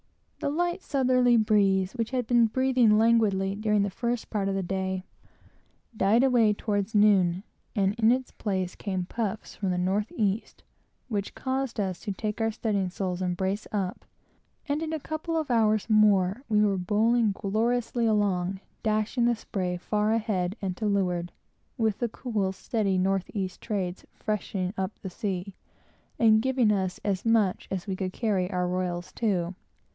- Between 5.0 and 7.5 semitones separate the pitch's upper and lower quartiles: No, average, 3.2 semitones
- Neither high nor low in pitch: No, high, 210 Hz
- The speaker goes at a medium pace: Yes, average, 170 wpm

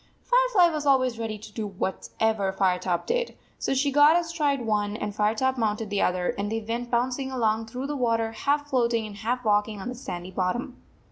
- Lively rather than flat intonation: No, average, 4.2 semitones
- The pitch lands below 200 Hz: No, high, 230 Hz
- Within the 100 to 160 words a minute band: No, average, 200 wpm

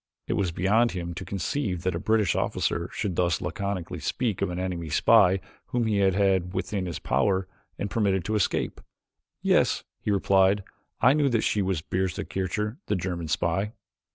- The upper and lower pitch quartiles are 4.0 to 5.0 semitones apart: No, average, 2.9 semitones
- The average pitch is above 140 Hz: No, very low, 95 Hz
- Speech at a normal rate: Yes, average, 180 wpm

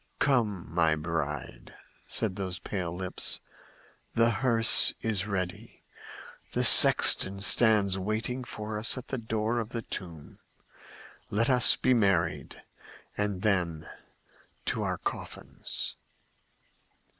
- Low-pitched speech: Yes, low, 100 Hz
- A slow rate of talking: Yes, slow, 110 wpm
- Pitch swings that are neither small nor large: Yes, average, 4.1 semitones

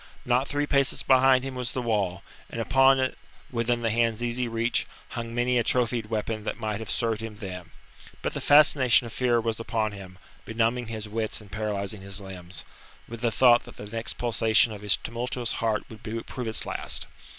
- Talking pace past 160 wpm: Yes, average, 195 wpm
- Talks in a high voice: No, low, 115 Hz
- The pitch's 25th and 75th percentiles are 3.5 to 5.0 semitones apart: No, narrow, 2.4 semitones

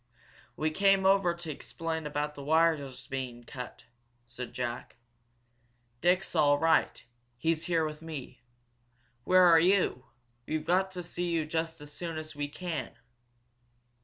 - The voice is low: No, medium, 160 Hz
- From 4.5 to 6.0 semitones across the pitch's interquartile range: No, average, 3.1 semitones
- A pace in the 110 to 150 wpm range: Yes, average, 140 wpm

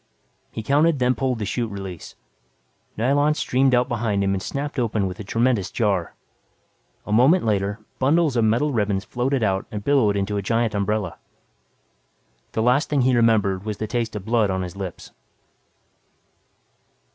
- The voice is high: No, low, 110 Hz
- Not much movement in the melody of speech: No, average, 4.2 semitones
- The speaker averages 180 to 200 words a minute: No, average, 165 wpm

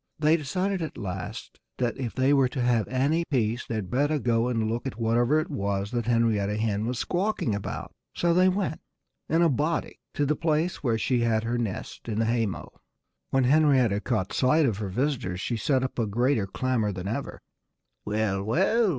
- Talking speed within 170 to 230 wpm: Yes, average, 195 wpm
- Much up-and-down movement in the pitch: No, average, 5.0 semitones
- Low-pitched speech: Yes, low, 120 Hz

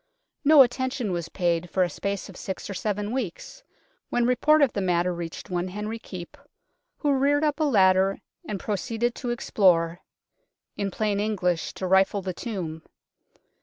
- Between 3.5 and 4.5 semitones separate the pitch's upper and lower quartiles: No, average, 5.0 semitones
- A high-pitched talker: Yes, high, 200 Hz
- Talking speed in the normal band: Yes, average, 165 wpm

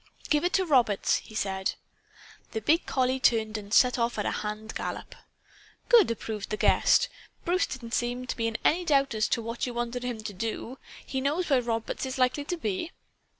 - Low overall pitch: No, high, 240 Hz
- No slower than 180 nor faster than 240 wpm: Yes, average, 200 wpm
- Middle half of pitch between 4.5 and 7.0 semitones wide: No, average, 3.7 semitones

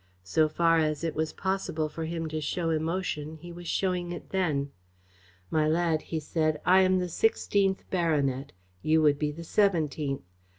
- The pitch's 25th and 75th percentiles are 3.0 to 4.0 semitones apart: No, narrow, 2.4 semitones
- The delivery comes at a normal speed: Yes, average, 170 wpm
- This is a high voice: No, medium, 160 Hz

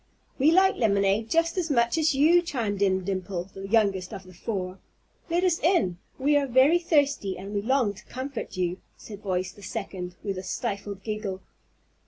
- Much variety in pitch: Yes, wide, 6.8 semitones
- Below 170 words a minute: No, average, 185 wpm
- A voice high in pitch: Yes, high, 210 Hz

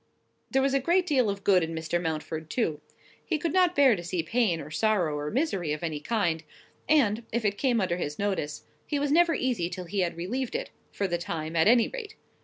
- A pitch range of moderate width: No, wide, 8.2 semitones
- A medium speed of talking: No, fast, 225 wpm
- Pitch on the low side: No, high, 200 Hz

